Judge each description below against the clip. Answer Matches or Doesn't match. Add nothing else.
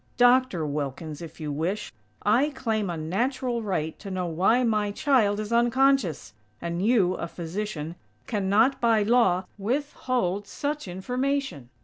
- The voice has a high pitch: Matches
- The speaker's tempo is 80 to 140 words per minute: Matches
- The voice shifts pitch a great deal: Matches